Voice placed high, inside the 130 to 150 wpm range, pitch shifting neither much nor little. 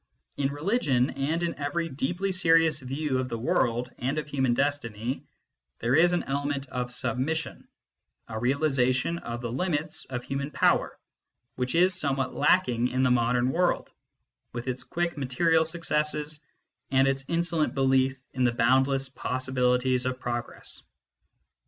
No: low, 135 Hz; average, 145 wpm; average, 3.6 semitones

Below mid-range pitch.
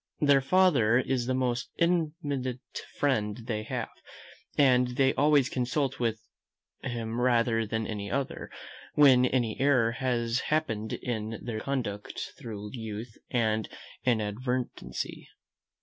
Yes: low, 125 Hz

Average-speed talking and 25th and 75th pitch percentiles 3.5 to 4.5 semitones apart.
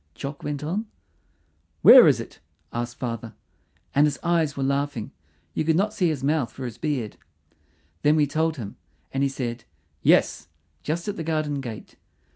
Yes: average, 170 wpm; average, 3.8 semitones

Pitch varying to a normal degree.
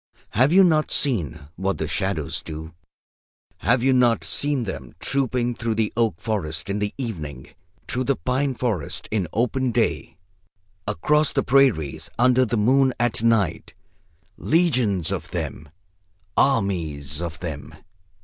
No: wide, 7.1 semitones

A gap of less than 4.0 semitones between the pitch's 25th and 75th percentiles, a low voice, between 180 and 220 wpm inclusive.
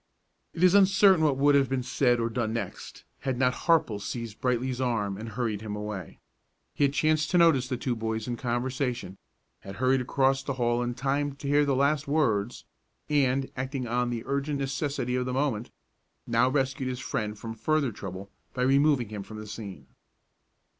Yes: average, 3.5 semitones; low, 125 Hz; average, 190 wpm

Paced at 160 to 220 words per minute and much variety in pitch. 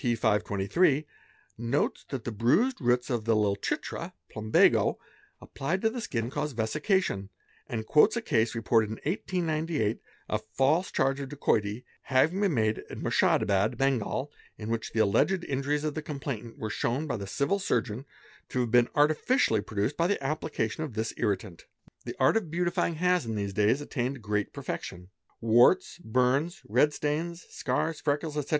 Yes: average, 165 wpm; wide, 5.9 semitones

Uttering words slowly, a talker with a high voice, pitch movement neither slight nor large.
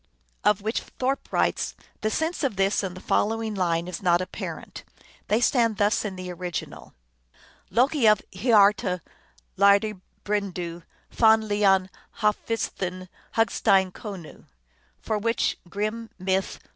Yes: slow, 130 wpm; high, 205 Hz; average, 3.0 semitones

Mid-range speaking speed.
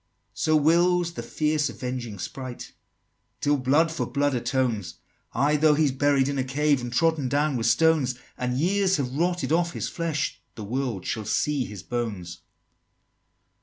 Yes: average, 165 wpm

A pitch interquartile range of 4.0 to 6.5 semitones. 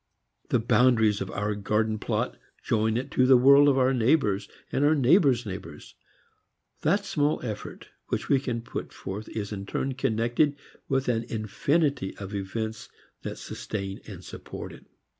Yes: average, 4.4 semitones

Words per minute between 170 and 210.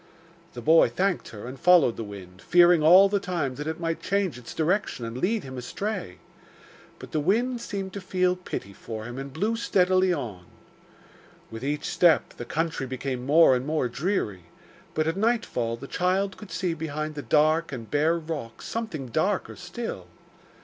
Yes: average, 175 wpm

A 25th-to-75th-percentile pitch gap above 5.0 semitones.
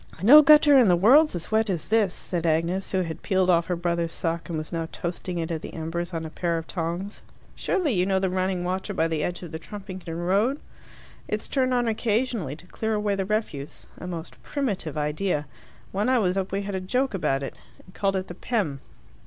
No: average, 4.0 semitones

